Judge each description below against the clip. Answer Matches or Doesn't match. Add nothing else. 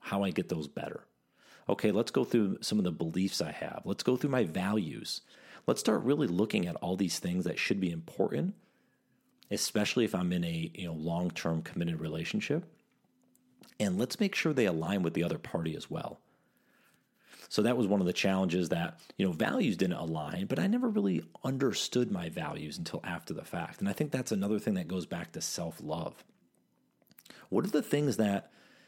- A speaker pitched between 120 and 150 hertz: Doesn't match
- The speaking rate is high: Doesn't match